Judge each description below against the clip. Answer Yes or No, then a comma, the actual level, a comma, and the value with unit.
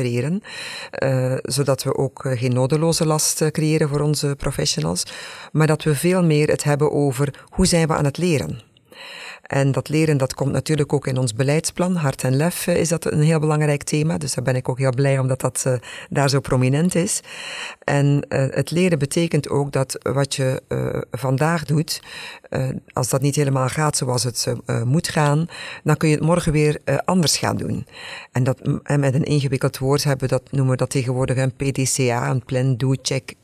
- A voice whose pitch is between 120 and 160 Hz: Yes, medium, 140 Hz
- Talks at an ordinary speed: Yes, average, 185 wpm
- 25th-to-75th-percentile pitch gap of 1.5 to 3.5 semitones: Yes, average, 2.8 semitones